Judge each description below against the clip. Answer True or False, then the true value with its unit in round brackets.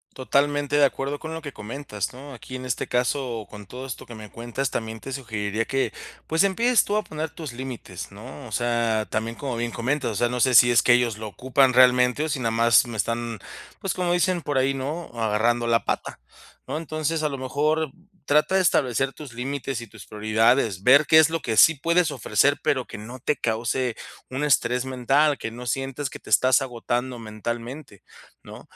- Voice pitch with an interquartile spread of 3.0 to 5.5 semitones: True (3.7 semitones)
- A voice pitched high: False (130 Hz)